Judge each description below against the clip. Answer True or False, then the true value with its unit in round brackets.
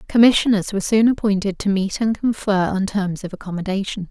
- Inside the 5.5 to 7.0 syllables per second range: True (5.9 syllables/s)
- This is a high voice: True (200 Hz)